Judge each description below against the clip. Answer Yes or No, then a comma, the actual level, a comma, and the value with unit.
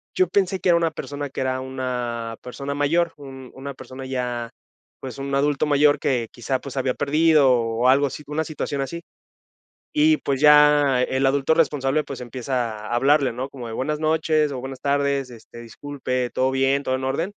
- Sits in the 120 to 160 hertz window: Yes, low, 135 Hz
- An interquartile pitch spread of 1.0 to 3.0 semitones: Yes, narrow, 2.5 semitones